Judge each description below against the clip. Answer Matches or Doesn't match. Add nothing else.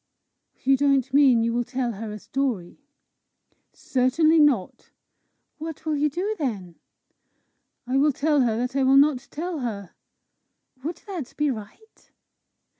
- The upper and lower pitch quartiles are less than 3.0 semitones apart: Doesn't match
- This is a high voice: Matches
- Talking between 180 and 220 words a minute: Doesn't match